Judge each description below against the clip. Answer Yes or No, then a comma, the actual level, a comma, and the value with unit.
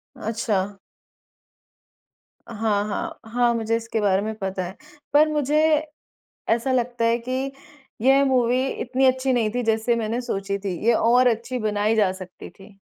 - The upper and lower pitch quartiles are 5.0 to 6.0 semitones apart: No, average, 3.4 semitones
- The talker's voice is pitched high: Yes, high, 230 Hz